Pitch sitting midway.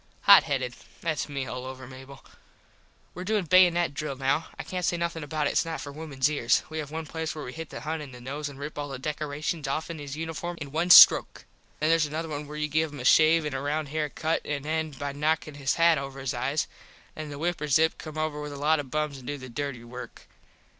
Yes: medium, 150 Hz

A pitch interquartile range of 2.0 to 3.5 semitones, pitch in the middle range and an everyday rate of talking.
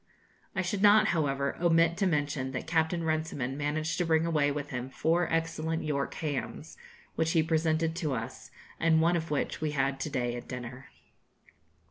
Yes: average, 2.9 semitones; medium, 155 Hz; average, 175 wpm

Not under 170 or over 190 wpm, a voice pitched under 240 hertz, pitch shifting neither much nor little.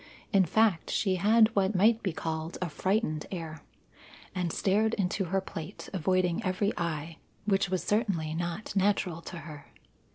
No: average, 155 wpm; medium, 185 Hz; average, 3.5 semitones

